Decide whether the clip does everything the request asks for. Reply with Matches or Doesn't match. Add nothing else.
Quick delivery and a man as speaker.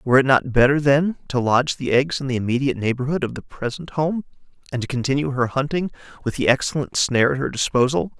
Matches